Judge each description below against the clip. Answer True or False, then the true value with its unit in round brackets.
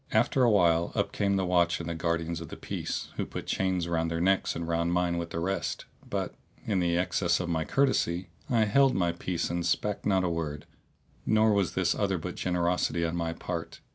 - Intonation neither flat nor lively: False (2.3 semitones)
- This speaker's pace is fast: True (210 wpm)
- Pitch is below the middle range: True (85 Hz)